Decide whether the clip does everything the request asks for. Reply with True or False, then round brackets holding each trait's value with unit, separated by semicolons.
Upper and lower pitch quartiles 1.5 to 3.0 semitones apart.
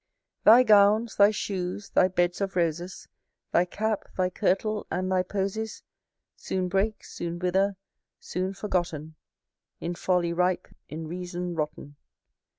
True (2.4 semitones)